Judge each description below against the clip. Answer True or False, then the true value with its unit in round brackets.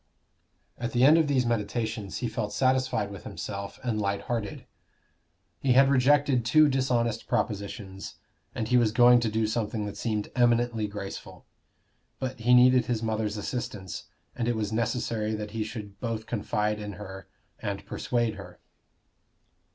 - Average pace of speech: True (155 wpm)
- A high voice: False (115 Hz)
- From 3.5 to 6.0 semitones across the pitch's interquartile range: False (2.7 semitones)